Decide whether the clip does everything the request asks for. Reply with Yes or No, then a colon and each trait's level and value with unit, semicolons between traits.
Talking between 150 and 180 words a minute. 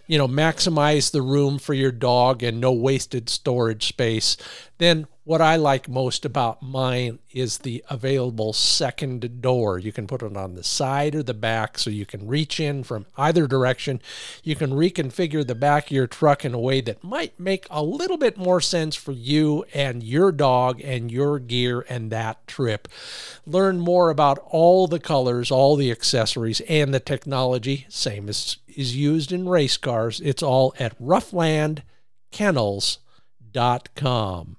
Yes: average, 165 wpm